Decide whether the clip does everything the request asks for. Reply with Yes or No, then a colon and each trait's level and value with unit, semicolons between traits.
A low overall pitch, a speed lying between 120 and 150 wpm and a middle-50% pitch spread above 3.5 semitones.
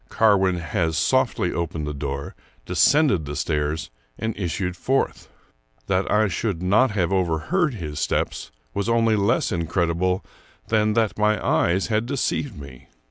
Yes: very low, 95 Hz; average, 140 wpm; average, 5.1 semitones